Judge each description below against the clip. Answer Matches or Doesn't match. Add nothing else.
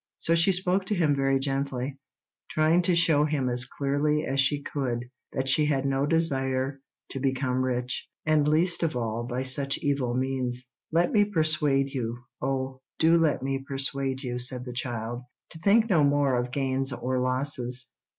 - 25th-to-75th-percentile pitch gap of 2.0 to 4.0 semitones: Matches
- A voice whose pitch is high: Doesn't match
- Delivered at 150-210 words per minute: Matches